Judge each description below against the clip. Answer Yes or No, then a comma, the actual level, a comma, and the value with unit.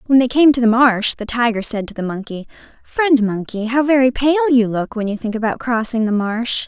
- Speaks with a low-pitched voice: No, high, 240 Hz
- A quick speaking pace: Yes, fast, 235 wpm